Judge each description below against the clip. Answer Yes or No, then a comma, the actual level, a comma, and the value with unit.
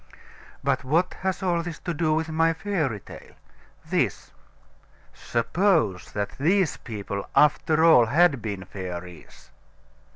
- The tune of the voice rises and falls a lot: Yes, wide, 8.2 semitones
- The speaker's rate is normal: No, slow, 125 wpm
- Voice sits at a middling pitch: Yes, medium, 155 Hz